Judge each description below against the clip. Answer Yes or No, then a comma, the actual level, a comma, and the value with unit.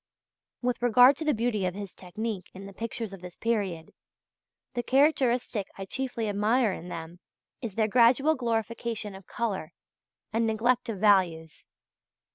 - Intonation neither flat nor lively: Yes, average, 3.9 semitones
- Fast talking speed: No, average, 150 wpm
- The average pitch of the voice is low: No, high, 220 Hz